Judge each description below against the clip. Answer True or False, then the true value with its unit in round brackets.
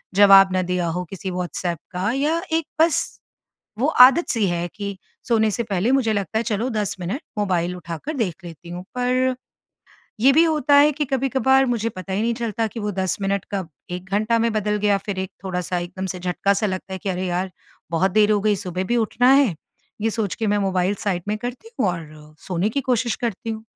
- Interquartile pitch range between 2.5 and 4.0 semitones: False (4.4 semitones)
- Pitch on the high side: True (205 Hz)